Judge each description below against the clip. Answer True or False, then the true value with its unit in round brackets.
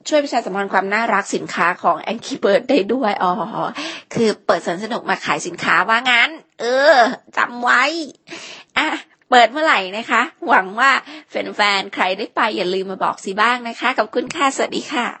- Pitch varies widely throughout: False (4.8 semitones)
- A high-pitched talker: True (235 Hz)